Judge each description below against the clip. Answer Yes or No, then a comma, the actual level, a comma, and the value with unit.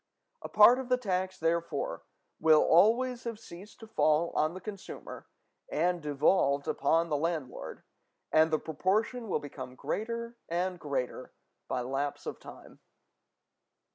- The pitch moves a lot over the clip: Yes, wide, 6.1 semitones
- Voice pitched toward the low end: No, medium, 170 Hz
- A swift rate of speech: No, average, 140 wpm